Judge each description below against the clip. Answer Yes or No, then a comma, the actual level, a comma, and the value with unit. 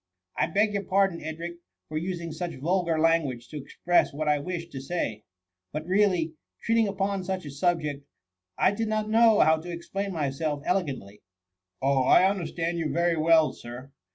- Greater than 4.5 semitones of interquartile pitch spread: No, average, 3.9 semitones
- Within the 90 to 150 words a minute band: No, average, 175 wpm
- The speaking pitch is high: No, medium, 170 Hz